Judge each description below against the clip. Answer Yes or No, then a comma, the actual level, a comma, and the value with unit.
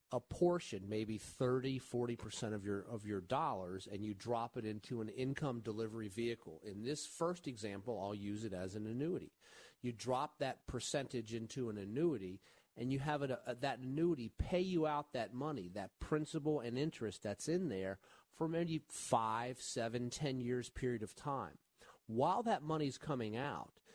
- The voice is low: Yes, low, 120 Hz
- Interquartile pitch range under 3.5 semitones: No, average, 4.9 semitones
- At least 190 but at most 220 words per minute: No, average, 175 wpm